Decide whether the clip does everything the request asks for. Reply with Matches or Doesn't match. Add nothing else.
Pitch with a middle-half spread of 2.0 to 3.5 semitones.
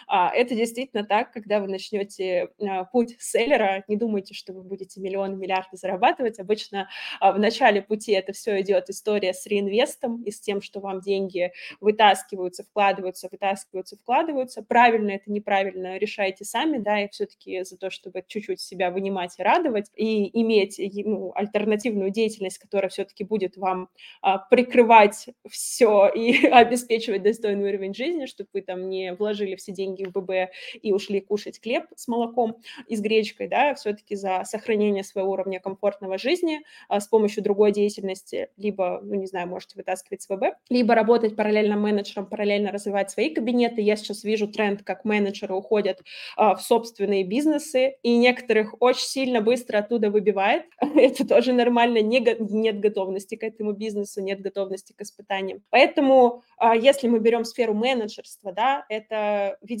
Matches